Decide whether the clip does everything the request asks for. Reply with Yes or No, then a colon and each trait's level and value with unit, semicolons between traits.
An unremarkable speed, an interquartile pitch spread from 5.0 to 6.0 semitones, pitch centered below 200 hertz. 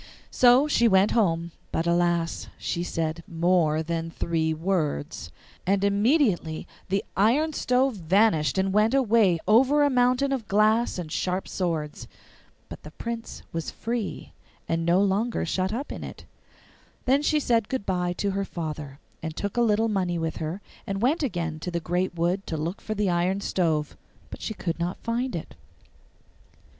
Yes: average, 170 wpm; average, 5.3 semitones; high, 190 Hz